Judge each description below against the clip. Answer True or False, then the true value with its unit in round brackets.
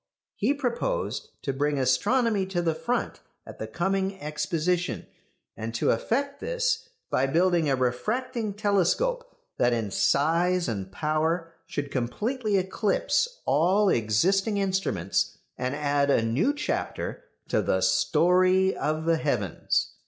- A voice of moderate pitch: True (180 Hz)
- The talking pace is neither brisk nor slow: False (130 wpm)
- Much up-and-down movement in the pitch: True (6.9 semitones)